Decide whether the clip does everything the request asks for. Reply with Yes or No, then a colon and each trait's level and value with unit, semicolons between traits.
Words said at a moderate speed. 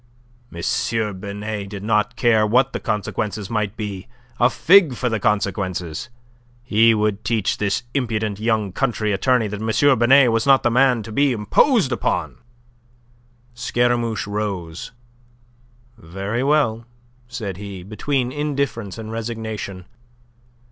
No: slow, 125 wpm